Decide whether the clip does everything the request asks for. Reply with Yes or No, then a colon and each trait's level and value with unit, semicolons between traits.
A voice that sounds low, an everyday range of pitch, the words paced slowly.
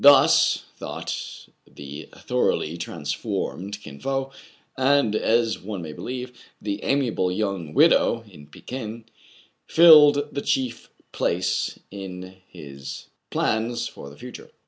No: low, 105 Hz; wide, 7.2 semitones; slow, 115 wpm